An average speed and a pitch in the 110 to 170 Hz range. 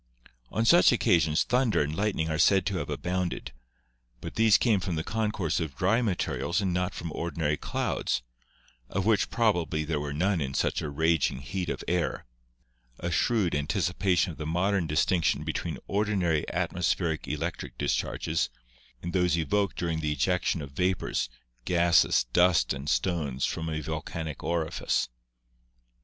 No: average, 160 wpm; very low, 85 Hz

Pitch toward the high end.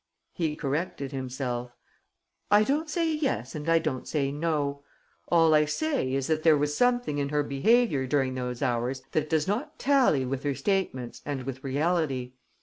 No: medium, 145 Hz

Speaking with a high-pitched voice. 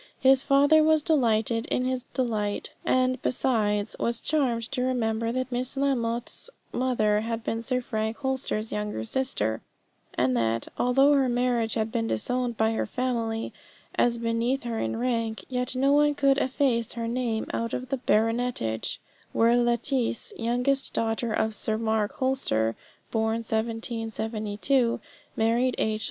Yes: high, 235 Hz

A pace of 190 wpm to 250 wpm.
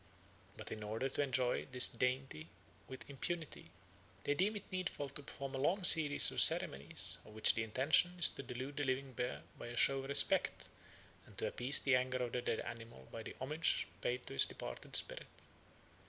Yes: average, 195 wpm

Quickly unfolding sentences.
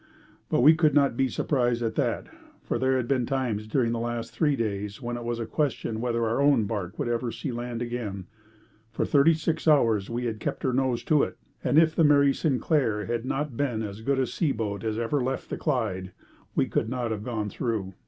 Yes: fast, 220 wpm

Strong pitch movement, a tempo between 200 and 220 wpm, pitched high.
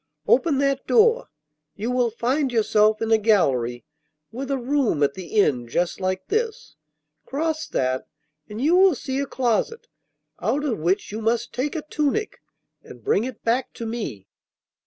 No: wide, 5.8 semitones; average, 165 wpm; high, 240 Hz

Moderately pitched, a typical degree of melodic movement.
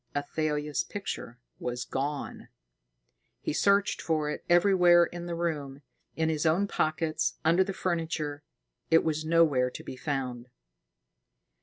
Yes: medium, 155 Hz; average, 3.0 semitones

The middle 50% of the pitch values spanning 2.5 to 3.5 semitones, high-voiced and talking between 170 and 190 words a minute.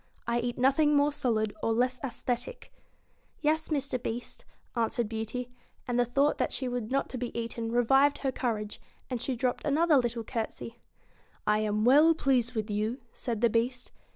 Yes: average, 2.9 semitones; high, 245 Hz; average, 180 wpm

